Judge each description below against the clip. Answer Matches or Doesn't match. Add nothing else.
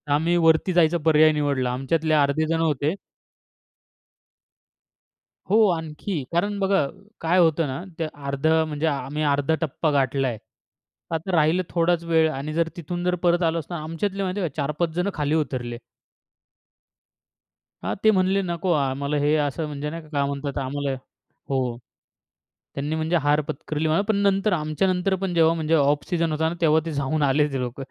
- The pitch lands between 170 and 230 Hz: Doesn't match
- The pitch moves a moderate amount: Matches